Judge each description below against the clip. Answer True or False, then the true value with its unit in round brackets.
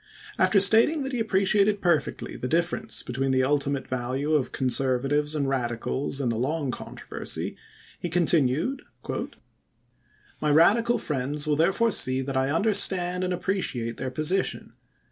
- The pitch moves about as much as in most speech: False (6.3 semitones)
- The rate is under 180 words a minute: True (145 wpm)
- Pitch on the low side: False (150 Hz)